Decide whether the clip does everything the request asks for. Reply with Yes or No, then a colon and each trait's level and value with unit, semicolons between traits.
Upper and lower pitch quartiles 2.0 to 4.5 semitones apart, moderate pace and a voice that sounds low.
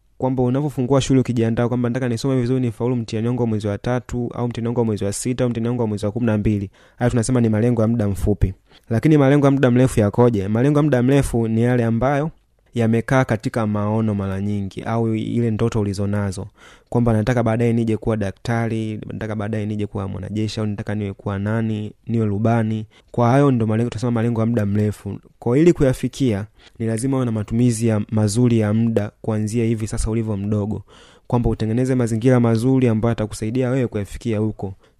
No: narrow, 2.5 semitones; fast, 165 wpm; low, 115 Hz